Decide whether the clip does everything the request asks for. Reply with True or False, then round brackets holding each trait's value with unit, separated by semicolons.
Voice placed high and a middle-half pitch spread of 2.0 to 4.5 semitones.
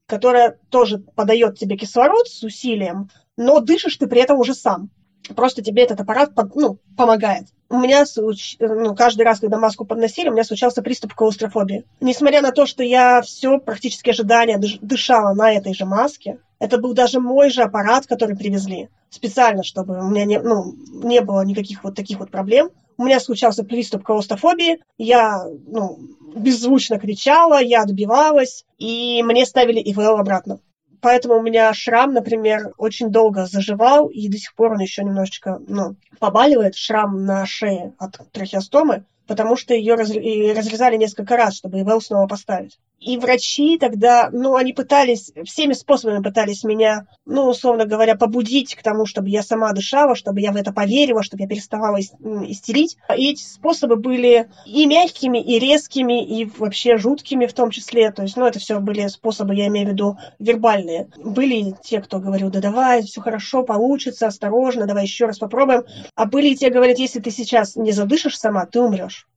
True (225 Hz; 3.2 semitones)